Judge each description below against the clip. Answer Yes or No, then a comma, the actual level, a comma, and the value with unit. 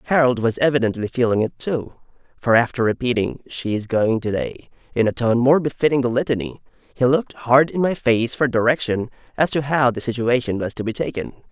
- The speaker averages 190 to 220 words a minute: Yes, average, 195 wpm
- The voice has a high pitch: No, low, 125 Hz